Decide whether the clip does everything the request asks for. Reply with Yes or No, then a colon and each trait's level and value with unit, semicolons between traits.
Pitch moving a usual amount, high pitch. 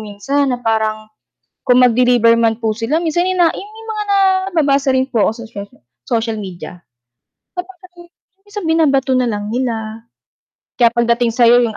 No: wide, 5.9 semitones; high, 245 Hz